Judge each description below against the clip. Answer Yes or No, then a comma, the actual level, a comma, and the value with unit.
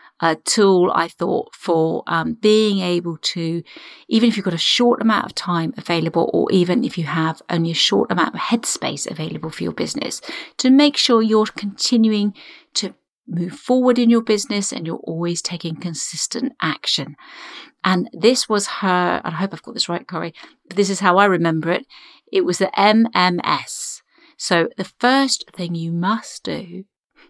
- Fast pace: No, average, 180 wpm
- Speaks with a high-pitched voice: Yes, high, 200 Hz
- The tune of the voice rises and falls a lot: Yes, wide, 5.8 semitones